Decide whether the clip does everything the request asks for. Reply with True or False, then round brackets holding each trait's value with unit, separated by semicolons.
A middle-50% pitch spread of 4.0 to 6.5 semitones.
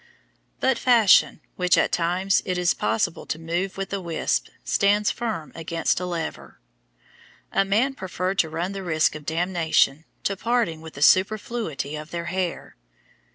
False (3.3 semitones)